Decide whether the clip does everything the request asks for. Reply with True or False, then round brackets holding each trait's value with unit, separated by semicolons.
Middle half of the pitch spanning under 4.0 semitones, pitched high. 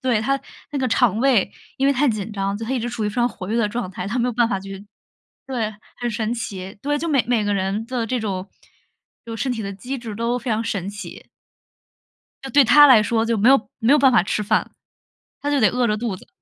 True (3.4 semitones; 230 Hz)